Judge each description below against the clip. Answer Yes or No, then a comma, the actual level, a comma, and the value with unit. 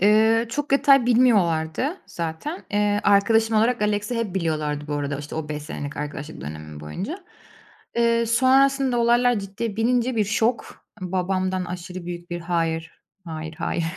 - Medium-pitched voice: No, high, 200 Hz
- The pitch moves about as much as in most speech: No, wide, 6.3 semitones